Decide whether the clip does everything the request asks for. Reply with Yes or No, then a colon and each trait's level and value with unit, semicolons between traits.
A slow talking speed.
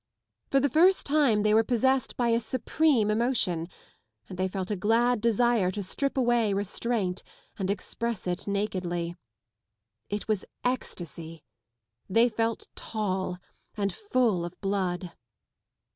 Yes: slow, 130 wpm